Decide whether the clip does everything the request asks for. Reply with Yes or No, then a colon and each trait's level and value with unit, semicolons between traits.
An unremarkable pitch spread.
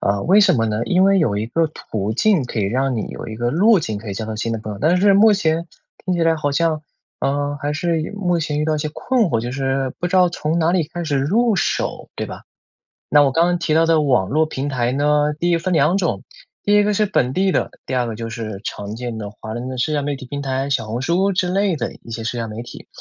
No: wide, 6.4 semitones